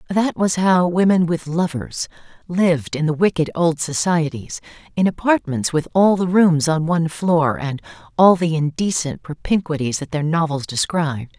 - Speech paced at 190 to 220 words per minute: No, average, 160 wpm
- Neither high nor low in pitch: Yes, medium, 165 Hz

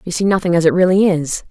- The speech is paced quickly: Yes, fast, 280 wpm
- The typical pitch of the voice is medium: Yes, medium, 180 Hz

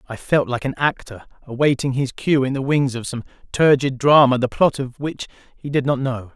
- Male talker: Yes, male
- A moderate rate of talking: No, fast, 215 wpm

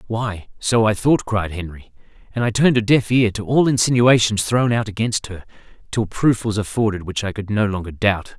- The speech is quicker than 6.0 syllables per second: No, 5.2 syllables/s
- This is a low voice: Yes, low, 110 Hz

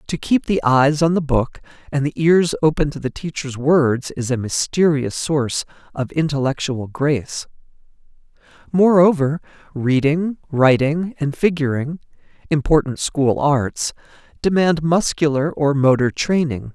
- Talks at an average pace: No, slow, 120 wpm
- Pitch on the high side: No, medium, 145 Hz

